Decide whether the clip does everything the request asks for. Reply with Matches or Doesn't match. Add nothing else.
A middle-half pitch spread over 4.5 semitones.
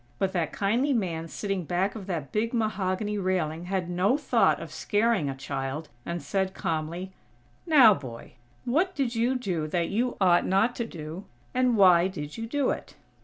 Matches